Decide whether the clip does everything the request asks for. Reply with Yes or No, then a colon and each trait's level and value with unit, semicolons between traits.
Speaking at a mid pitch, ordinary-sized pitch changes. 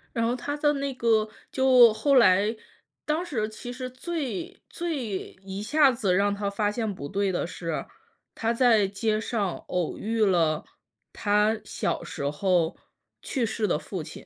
No: high, 220 Hz; average, 4.4 semitones